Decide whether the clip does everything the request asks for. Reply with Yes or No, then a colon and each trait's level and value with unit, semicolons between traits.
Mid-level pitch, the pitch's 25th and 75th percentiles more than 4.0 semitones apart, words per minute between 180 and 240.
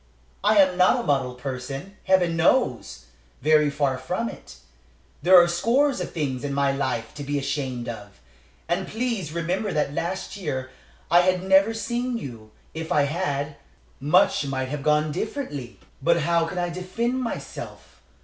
No: medium, 160 Hz; wide, 5.4 semitones; average, 160 wpm